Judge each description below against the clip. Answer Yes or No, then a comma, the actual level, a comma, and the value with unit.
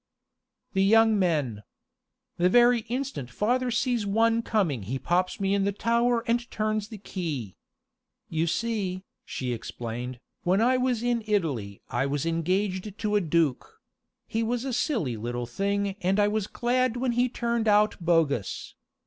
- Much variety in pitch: Yes, wide, 6.3 semitones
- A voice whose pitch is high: Yes, high, 200 Hz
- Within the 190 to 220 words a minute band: No, average, 155 wpm